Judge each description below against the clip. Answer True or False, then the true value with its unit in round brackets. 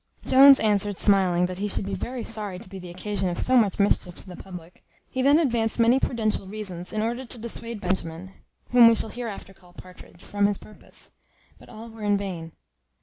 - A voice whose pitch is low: False (205 Hz)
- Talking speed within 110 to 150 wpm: False (205 wpm)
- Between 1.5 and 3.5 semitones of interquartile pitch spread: False (3.9 semitones)